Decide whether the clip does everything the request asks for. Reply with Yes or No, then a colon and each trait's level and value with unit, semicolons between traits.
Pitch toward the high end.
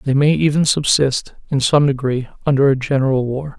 No: low, 135 Hz